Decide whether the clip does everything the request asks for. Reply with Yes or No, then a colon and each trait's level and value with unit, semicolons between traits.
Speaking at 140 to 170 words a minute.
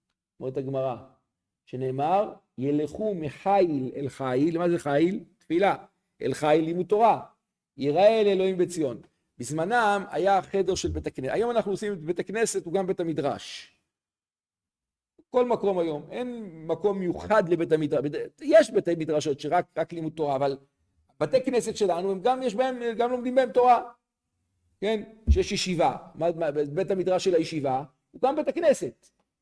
Yes: average, 145 wpm